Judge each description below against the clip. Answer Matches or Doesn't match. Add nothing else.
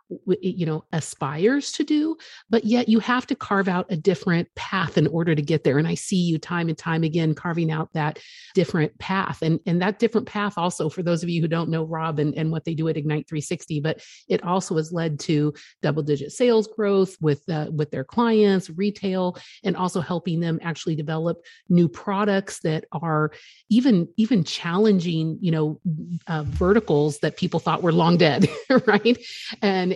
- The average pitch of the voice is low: Doesn't match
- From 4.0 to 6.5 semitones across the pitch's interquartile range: Doesn't match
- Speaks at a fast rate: Doesn't match